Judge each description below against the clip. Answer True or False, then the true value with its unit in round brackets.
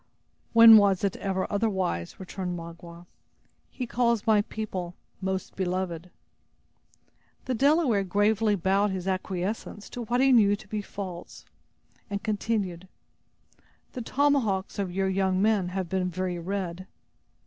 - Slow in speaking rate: True (130 wpm)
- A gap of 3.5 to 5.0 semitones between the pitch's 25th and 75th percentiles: False (2.9 semitones)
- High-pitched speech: True (195 Hz)